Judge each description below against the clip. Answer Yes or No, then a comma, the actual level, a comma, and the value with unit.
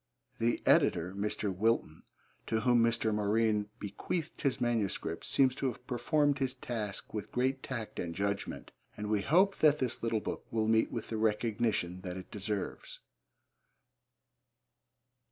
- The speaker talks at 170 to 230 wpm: No, average, 145 wpm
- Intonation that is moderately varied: Yes, average, 3.3 semitones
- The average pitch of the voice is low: Yes, low, 110 Hz